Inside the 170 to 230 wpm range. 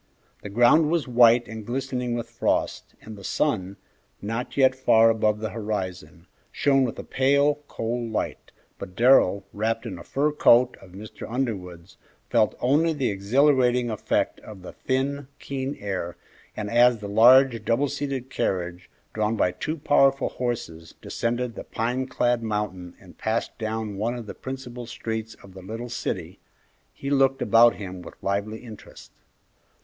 No: average, 160 wpm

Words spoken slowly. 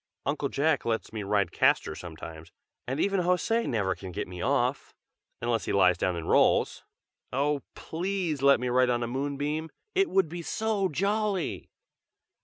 No: average, 165 wpm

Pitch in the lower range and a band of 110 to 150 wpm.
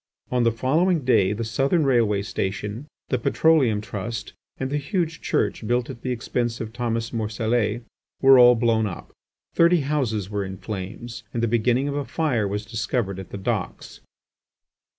No: low, 115 Hz; average, 170 wpm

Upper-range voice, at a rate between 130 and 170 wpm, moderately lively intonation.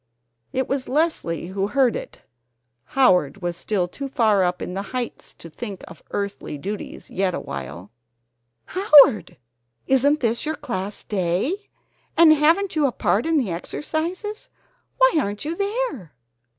No: high, 235 Hz; average, 140 wpm; wide, 8.7 semitones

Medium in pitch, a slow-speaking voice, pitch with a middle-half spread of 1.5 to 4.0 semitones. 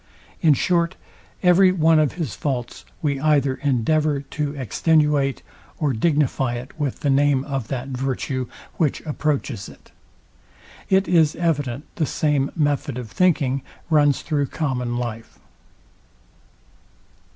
Yes: medium, 145 Hz; slow, 125 wpm; average, 2.9 semitones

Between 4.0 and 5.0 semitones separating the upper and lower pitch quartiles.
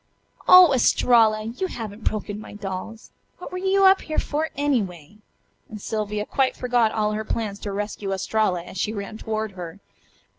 No: average, 3.4 semitones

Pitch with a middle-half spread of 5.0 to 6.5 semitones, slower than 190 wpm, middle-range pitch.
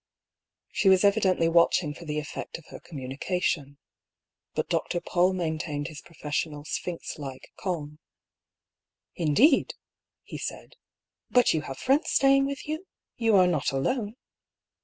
Yes: average, 5.3 semitones; average, 150 wpm; medium, 170 Hz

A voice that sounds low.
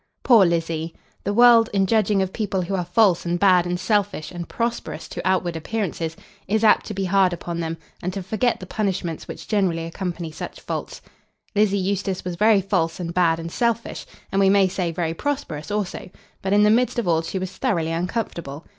No: medium, 185 Hz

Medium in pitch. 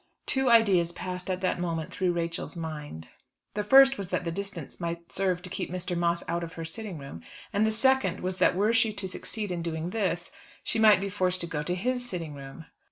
Yes: medium, 180 Hz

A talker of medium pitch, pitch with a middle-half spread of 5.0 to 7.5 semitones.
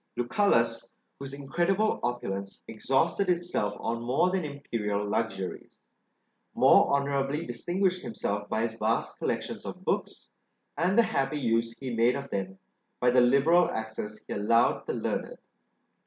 No: low, 125 Hz; wide, 5.4 semitones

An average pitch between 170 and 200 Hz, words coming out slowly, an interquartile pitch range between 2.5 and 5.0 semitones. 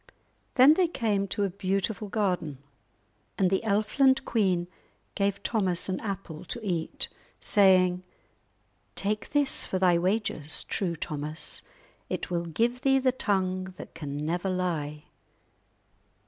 Yes: high, 190 Hz; slow, 130 wpm; average, 3.6 semitones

